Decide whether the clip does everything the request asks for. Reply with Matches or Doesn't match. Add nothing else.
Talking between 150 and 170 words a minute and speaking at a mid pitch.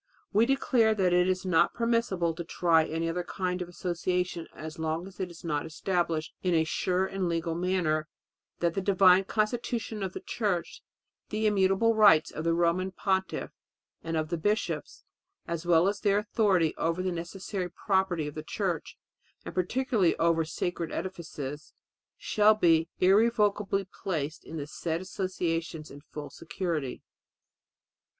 Matches